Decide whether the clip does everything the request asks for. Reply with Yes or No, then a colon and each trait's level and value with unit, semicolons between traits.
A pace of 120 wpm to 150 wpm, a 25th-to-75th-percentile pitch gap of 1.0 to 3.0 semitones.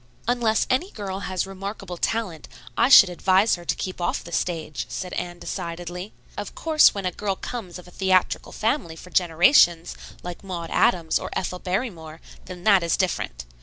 No: average, 175 wpm; narrow, 2.6 semitones